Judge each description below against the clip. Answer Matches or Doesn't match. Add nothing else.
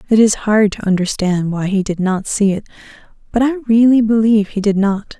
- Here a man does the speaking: Doesn't match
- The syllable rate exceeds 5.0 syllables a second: Matches